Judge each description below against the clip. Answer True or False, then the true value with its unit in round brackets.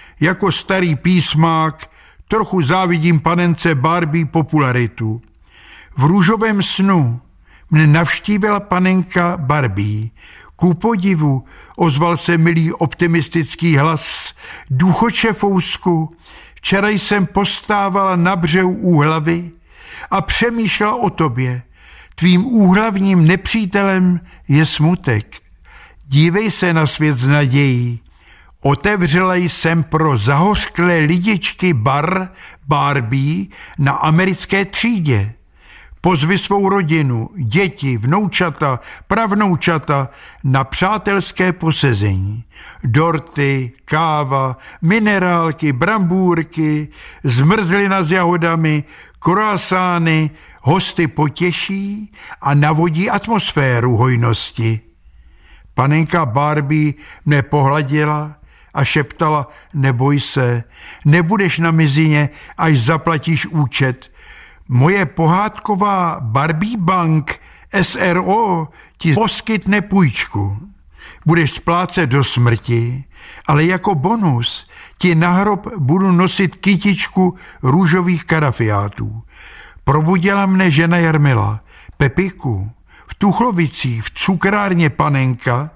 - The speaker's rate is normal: False (85 wpm)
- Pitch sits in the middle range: True (165 Hz)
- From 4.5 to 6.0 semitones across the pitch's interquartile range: True (4.8 semitones)